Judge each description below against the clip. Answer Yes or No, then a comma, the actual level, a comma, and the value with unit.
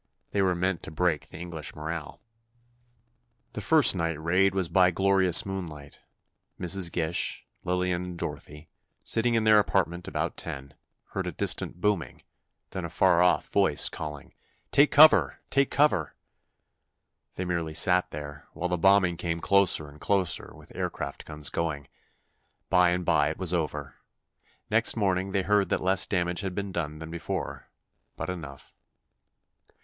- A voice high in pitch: No, very low, 90 Hz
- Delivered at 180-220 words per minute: No, average, 150 wpm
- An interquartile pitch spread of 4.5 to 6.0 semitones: No, average, 3.2 semitones